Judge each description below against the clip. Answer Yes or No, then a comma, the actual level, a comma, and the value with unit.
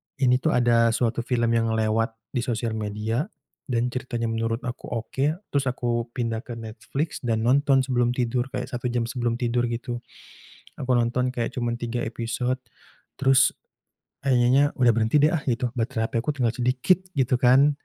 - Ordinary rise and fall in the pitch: No, narrow, 1.9 semitones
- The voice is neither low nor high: No, low, 120 Hz